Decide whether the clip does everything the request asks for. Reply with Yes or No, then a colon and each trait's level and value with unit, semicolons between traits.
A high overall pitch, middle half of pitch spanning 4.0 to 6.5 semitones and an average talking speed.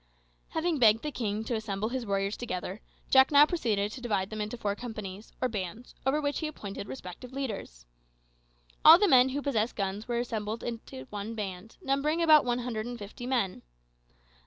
Yes: high, 230 Hz; average, 4.4 semitones; average, 185 wpm